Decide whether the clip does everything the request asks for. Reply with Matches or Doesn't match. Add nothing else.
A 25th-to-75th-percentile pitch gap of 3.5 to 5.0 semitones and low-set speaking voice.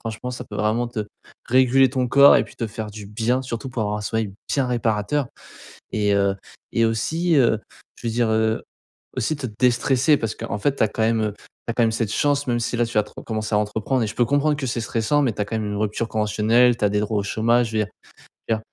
Doesn't match